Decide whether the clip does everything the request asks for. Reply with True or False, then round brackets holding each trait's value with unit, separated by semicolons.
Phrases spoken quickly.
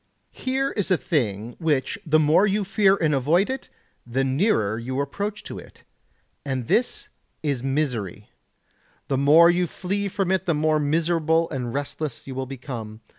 False (165 wpm)